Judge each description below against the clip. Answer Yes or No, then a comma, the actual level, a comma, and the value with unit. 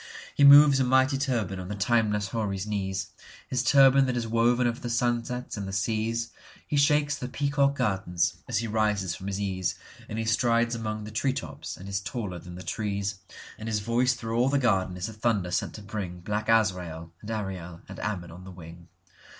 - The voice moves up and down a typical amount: Yes, average, 4.0 semitones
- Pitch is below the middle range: Yes, low, 110 Hz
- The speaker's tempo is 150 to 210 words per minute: Yes, average, 190 wpm